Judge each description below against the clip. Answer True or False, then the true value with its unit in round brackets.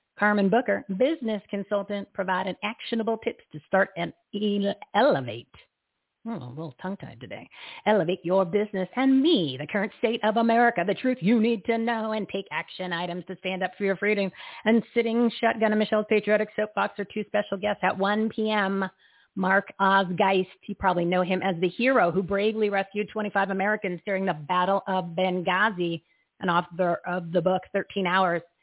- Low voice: False (200 Hz)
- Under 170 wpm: False (175 wpm)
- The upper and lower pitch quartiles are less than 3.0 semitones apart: True (2.5 semitones)